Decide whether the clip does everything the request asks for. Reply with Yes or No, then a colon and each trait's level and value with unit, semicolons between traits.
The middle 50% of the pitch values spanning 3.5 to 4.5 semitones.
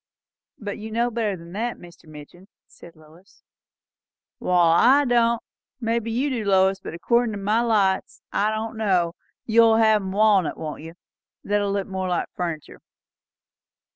Yes: average, 4.1 semitones